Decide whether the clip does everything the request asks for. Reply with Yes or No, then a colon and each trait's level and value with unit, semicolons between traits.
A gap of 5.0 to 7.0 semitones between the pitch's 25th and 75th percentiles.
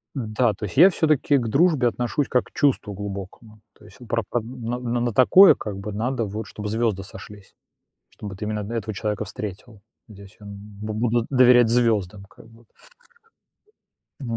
No: average, 2.9 semitones